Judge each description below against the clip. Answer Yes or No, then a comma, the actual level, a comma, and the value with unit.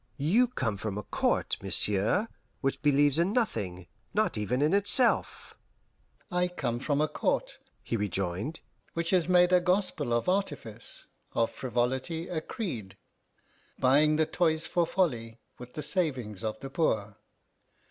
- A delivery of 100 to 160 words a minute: Yes, average, 145 wpm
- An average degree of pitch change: No, wide, 7.6 semitones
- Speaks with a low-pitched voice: No, medium, 145 Hz